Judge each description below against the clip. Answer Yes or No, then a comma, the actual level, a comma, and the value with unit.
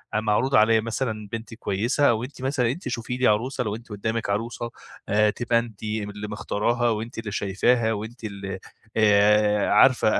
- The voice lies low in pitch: Yes, low, 110 Hz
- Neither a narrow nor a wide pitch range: No, narrow, 2.3 semitones